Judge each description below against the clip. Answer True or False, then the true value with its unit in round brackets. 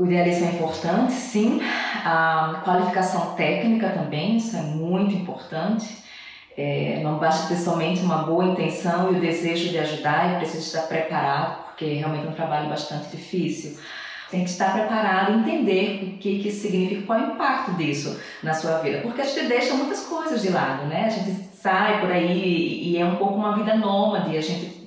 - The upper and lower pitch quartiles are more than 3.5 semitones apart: True (4.3 semitones)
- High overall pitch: False (180 Hz)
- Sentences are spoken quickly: True (190 wpm)